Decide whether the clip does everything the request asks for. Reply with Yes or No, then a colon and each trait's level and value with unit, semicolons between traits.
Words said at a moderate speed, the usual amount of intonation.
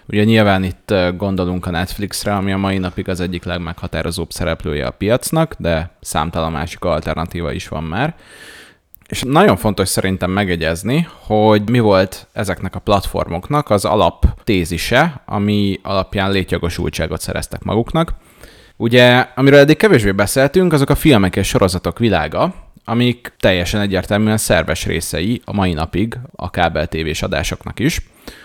Yes: average, 135 wpm; average, 4.2 semitones